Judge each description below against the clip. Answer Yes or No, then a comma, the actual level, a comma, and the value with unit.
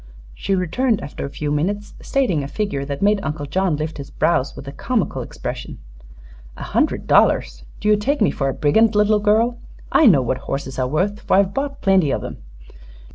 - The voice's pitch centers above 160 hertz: Yes, high, 190 Hz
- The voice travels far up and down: Yes, wide, 6.9 semitones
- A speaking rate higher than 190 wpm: Yes, average, 200 wpm